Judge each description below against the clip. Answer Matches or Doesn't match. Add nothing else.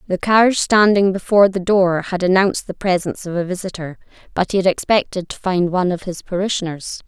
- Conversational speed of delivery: Matches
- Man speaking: Doesn't match